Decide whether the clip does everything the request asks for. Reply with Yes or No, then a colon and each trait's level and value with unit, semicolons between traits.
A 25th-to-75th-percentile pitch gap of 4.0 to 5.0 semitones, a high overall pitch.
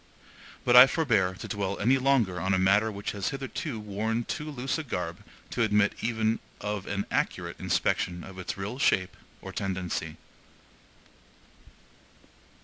No: average, 4.4 semitones; low, 105 Hz